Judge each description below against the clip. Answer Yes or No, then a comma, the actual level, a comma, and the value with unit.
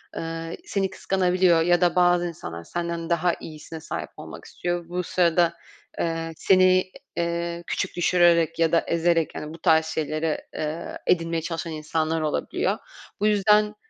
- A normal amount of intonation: No, narrow, 1.4 semitones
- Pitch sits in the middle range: Yes, medium, 170 Hz